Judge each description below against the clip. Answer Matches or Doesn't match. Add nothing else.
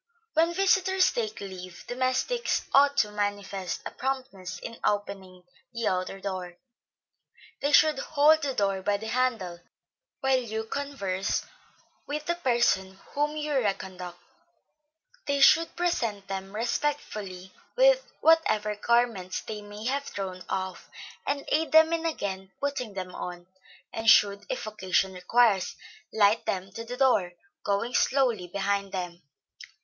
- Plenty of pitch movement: Matches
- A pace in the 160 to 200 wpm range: Doesn't match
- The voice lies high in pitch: Matches